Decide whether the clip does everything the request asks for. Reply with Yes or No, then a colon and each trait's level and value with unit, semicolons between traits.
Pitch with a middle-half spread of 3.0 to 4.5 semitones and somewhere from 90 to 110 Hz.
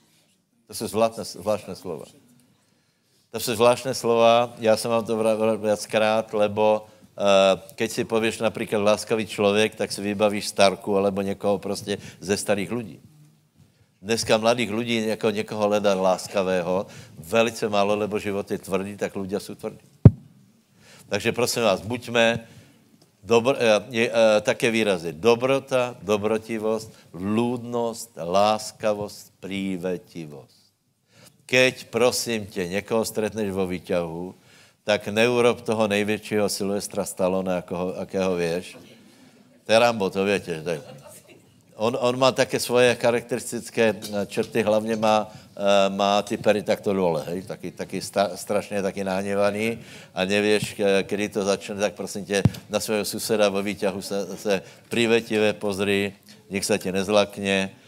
No: narrow, 2.4 semitones; low, 105 Hz